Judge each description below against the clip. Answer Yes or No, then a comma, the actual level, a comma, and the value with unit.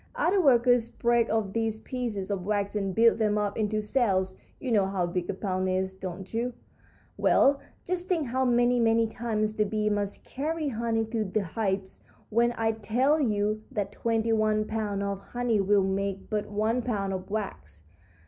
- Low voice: No, high, 215 Hz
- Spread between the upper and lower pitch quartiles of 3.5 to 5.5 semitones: No, average, 2.9 semitones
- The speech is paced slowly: No, average, 180 wpm